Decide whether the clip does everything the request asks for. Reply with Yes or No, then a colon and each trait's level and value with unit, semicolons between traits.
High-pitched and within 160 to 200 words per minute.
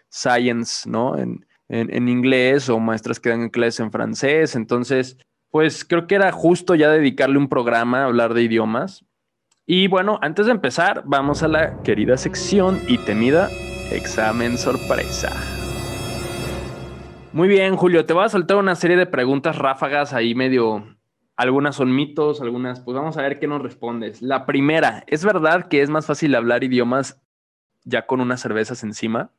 No: low, 130 Hz; average, 165 wpm